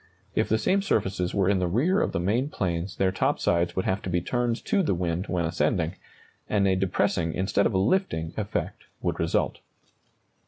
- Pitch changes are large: No, average, 3.5 semitones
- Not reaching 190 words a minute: No, average, 200 wpm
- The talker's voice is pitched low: Yes, very low, 95 Hz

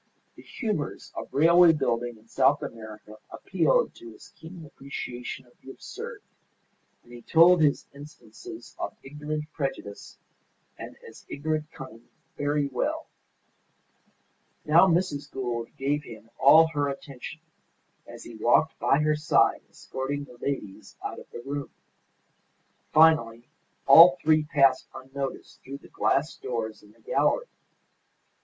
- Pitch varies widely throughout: No, average, 4.2 semitones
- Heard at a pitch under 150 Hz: Yes, medium, 140 Hz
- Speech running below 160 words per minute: Yes, slow, 135 wpm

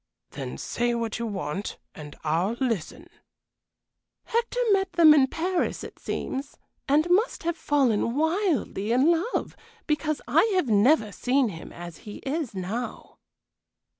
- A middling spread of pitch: No, wide, 7.7 semitones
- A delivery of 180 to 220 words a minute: No, slow, 135 wpm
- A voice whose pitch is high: Yes, very high, 265 Hz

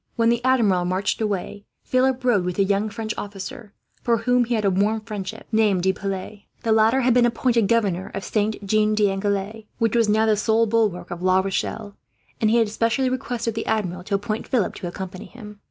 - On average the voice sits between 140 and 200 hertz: No, high, 215 Hz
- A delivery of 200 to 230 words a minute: Yes, fast, 205 wpm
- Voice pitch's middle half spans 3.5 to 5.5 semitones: No, narrow, 2.6 semitones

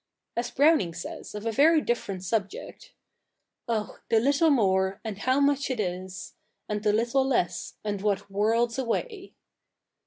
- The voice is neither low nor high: No, high, 225 Hz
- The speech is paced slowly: No, average, 155 wpm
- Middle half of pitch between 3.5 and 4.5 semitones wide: No, average, 5.3 semitones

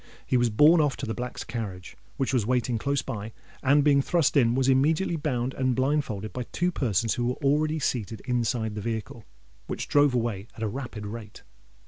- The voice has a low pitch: Yes, low, 125 Hz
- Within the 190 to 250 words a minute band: Yes, average, 195 wpm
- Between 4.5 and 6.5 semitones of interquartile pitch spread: No, average, 3.9 semitones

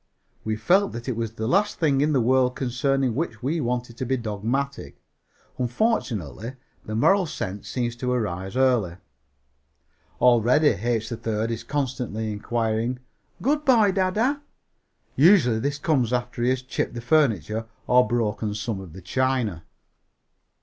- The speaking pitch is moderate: No, low, 120 Hz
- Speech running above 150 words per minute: No, average, 145 wpm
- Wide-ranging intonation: No, average, 3.7 semitones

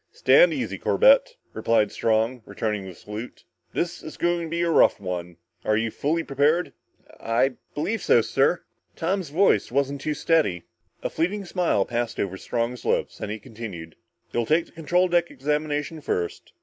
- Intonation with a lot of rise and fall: Yes, wide, 7.4 semitones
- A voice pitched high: No, medium, 140 Hz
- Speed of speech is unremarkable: Yes, average, 165 wpm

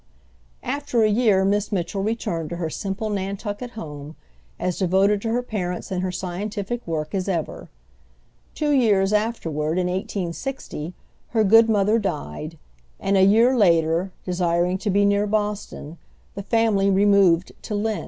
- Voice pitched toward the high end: Yes, high, 195 Hz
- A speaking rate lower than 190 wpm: Yes, average, 150 wpm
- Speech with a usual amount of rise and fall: Yes, average, 3.2 semitones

